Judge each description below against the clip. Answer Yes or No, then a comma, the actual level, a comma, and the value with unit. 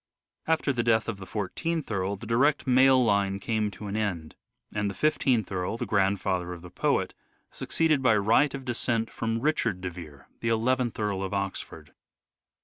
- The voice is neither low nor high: No, low, 110 Hz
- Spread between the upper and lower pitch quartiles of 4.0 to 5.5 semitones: Yes, average, 4.5 semitones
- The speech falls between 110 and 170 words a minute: No, average, 180 wpm